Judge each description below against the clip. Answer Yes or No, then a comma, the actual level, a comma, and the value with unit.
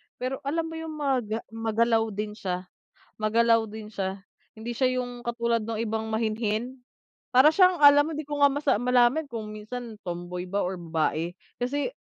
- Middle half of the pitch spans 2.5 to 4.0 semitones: Yes, average, 3.5 semitones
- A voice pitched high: Yes, high, 230 Hz